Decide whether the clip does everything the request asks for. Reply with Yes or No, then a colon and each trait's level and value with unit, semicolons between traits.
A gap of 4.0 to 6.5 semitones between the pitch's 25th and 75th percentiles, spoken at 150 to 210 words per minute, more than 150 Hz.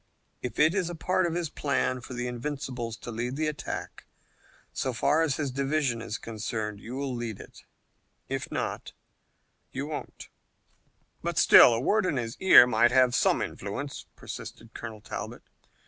No: average, 4.4 semitones; average, 160 wpm; low, 130 Hz